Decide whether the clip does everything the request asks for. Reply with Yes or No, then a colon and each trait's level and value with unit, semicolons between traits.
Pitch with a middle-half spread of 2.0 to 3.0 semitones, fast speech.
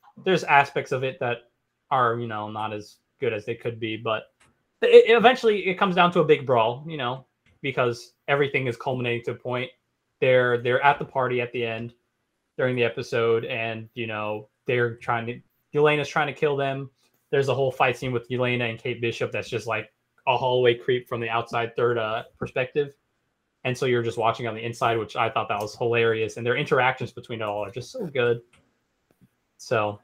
Yes: narrow, 2.6 semitones; fast, 210 wpm